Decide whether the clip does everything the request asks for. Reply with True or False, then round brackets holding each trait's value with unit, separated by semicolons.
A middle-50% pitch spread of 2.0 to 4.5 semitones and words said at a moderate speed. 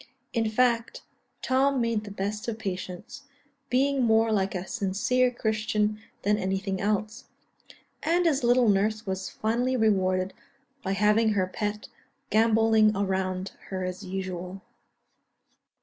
False (3.2 semitones; 125 wpm)